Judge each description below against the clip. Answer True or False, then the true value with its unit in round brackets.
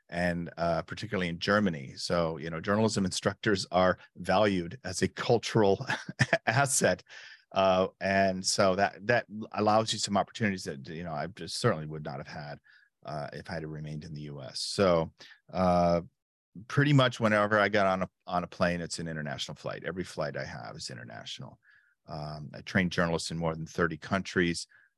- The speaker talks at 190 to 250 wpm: False (180 wpm)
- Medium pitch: False (90 Hz)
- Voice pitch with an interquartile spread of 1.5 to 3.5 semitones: False (3.9 semitones)